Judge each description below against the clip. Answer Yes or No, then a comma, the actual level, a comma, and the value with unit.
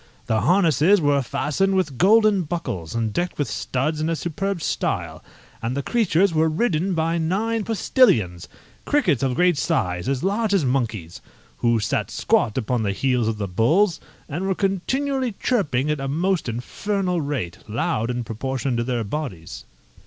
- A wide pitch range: Yes, wide, 8.2 semitones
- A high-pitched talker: No, medium, 150 Hz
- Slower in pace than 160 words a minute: No, average, 165 wpm